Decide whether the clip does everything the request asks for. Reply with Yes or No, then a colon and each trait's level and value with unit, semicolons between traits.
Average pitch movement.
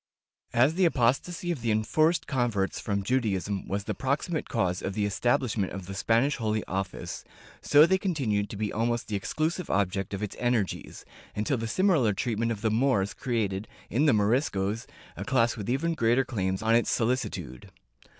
Yes: average, 4.5 semitones